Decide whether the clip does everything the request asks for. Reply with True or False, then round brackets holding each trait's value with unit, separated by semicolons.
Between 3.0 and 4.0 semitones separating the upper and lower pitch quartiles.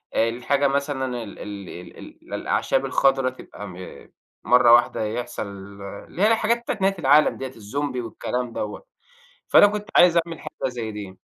False (5.0 semitones)